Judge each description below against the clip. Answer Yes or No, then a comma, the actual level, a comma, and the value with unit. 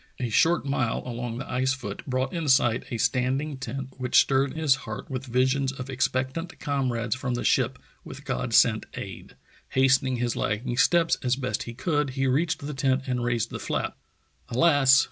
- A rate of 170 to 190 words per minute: Yes, average, 185 wpm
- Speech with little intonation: Yes, narrow, 2.0 semitones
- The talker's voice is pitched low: Yes, low, 130 Hz